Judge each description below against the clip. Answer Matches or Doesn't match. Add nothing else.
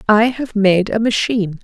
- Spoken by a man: Doesn't match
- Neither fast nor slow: Matches